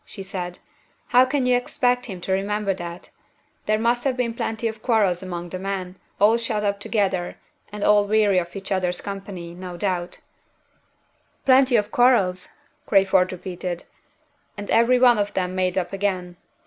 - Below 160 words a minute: No, average, 165 wpm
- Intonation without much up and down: No, average, 3.6 semitones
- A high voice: Yes, high, 200 Hz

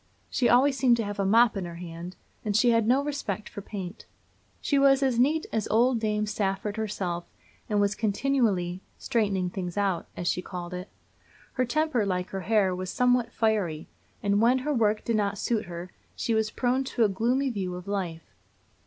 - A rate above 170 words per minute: Yes, average, 195 wpm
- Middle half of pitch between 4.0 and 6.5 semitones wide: Yes, average, 4.4 semitones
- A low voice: No, high, 210 Hz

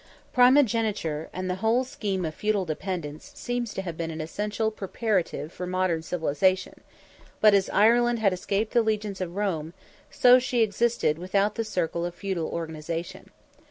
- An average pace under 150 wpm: No, average, 160 wpm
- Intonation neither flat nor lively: Yes, average, 4.5 semitones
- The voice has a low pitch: No, high, 190 Hz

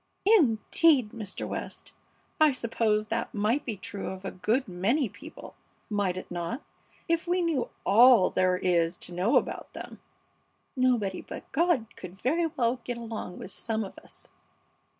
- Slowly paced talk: No, average, 155 wpm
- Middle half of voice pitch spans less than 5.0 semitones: No, average, 5.3 semitones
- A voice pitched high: Yes, high, 225 Hz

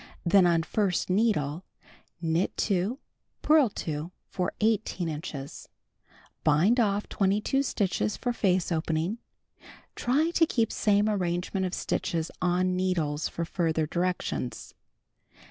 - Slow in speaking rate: Yes, slow, 115 wpm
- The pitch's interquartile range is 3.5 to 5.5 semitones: Yes, average, 4.2 semitones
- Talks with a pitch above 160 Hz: Yes, medium, 185 Hz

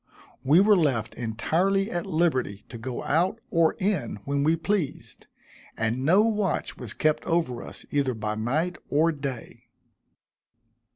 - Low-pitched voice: No, medium, 155 Hz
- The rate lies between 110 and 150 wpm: Yes, average, 140 wpm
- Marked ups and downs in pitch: Yes, wide, 6.0 semitones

